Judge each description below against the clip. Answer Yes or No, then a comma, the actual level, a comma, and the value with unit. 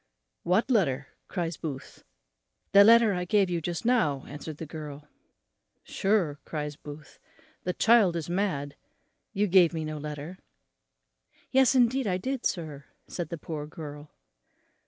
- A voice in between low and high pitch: Yes, medium, 170 Hz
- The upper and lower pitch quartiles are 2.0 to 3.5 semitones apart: No, average, 5.2 semitones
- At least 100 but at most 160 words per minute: Yes, average, 140 wpm